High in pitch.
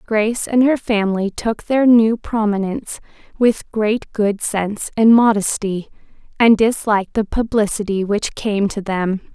Yes: high, 215 Hz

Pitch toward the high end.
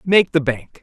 No: medium, 175 Hz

